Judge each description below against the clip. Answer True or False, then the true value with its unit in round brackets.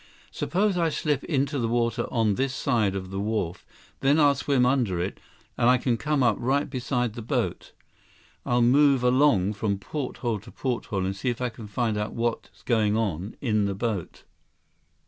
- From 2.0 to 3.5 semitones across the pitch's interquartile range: False (4.1 semitones)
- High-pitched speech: False (120 Hz)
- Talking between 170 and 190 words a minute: True (185 wpm)